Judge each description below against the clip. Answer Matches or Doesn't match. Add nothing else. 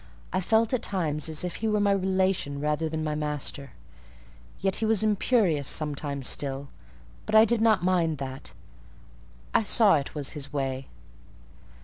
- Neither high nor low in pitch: Matches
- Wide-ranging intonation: Matches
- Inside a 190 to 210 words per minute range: Doesn't match